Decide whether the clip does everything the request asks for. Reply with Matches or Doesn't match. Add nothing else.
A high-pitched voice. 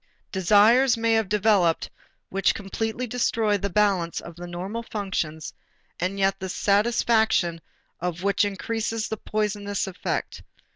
Matches